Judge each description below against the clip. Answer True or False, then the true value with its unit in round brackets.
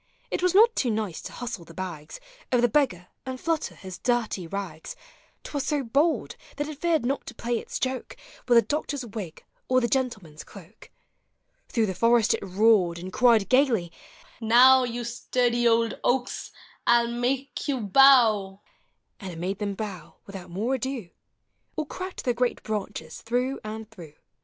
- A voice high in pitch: True (235 Hz)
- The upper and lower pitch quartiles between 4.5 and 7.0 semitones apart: True (4.8 semitones)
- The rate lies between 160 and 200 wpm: True (180 wpm)